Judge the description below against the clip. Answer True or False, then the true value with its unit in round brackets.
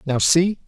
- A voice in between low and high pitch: True (160 Hz)